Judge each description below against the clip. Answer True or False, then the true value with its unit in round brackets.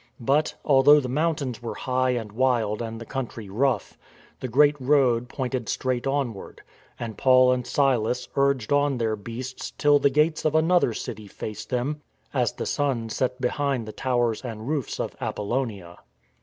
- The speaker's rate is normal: True (165 wpm)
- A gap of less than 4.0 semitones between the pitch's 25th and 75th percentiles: True (3.3 semitones)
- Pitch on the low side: True (125 Hz)